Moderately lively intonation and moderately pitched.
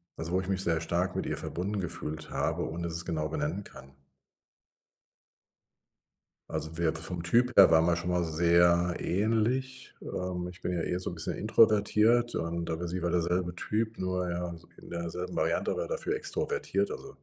No: average, 3.3 semitones; very low, 90 Hz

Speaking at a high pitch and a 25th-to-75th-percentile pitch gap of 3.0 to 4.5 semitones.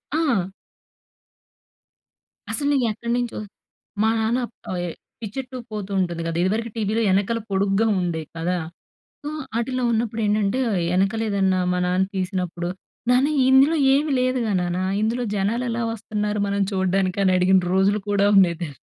Yes: high, 205 Hz; average, 3.7 semitones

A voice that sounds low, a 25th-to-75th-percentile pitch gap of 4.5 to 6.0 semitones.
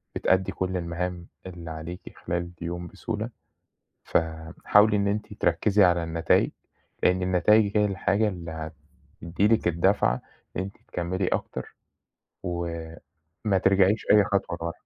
No: very low, 90 Hz; average, 3.0 semitones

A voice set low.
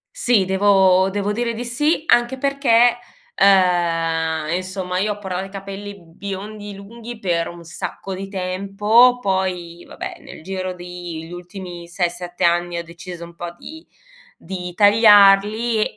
No: high, 190 Hz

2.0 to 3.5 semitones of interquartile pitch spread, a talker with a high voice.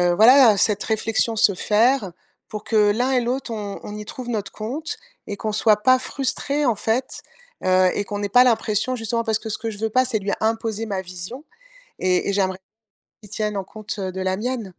Yes: average, 3.0 semitones; high, 215 Hz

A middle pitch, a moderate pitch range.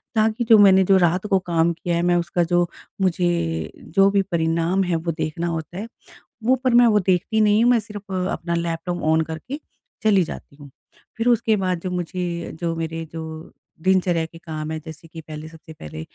Yes: medium, 175 Hz; average, 3.2 semitones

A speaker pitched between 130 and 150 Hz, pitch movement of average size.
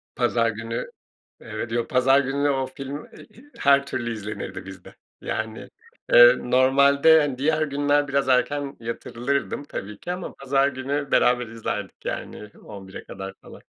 Yes: low, 135 Hz; average, 3.4 semitones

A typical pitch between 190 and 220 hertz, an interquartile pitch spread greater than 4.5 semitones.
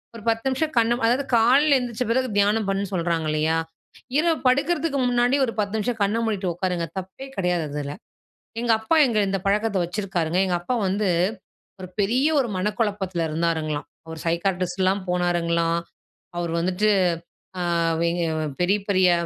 Yes: high, 195 Hz; average, 4.9 semitones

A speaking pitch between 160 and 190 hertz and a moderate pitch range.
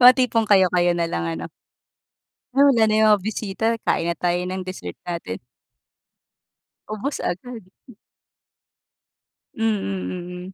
Yes: medium, 185 Hz; average, 4.1 semitones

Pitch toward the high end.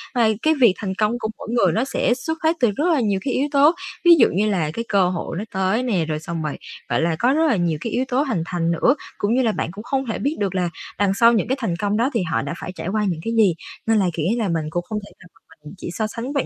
Yes: high, 215 Hz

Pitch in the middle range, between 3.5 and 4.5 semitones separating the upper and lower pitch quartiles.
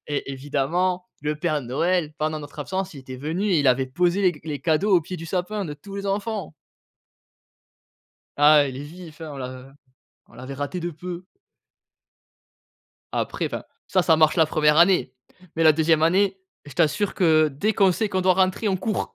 Yes: medium, 160 Hz; average, 4.1 semitones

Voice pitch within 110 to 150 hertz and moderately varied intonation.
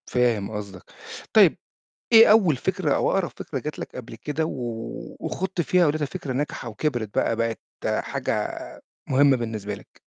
No: low, 135 Hz; wide, 5.8 semitones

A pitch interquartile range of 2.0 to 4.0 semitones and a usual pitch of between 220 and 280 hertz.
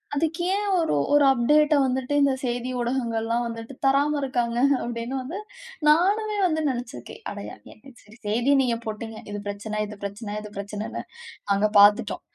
No: average, 4.6 semitones; high, 240 Hz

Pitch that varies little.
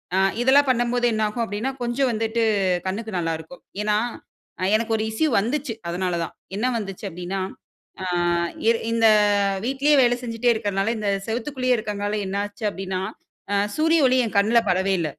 No: average, 3.6 semitones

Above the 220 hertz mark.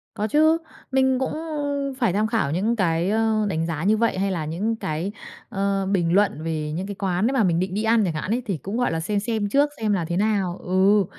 No: high, 200 Hz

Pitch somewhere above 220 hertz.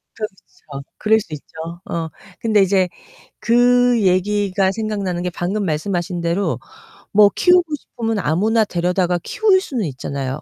No: high, 195 Hz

